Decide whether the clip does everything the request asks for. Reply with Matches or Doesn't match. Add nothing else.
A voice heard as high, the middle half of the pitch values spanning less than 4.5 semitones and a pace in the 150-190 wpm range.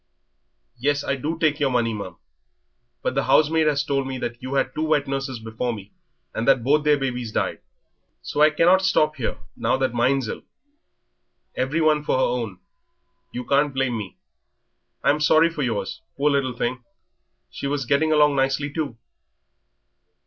Doesn't match